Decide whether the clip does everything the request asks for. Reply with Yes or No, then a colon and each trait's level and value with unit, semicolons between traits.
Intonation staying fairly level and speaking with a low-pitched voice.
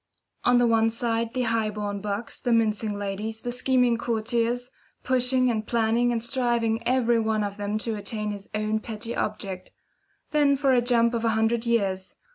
No: narrow, 2.1 semitones; high, 230 Hz